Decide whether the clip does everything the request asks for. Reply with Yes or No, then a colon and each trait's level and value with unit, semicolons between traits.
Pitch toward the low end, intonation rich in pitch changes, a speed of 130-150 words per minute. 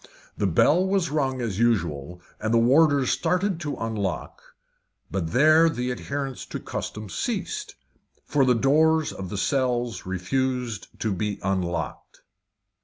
Yes: low, 125 Hz; wide, 7.0 semitones; slow, 135 wpm